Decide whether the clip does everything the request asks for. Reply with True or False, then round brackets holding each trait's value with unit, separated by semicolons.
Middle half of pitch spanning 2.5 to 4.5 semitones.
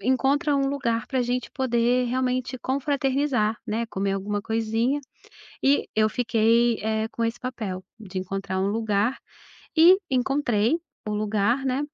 True (3.6 semitones)